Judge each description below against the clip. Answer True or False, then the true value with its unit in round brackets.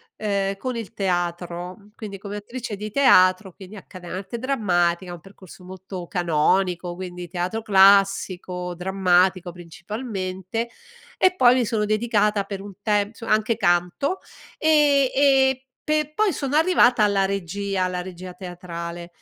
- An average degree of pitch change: True (3.9 semitones)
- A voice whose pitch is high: True (195 Hz)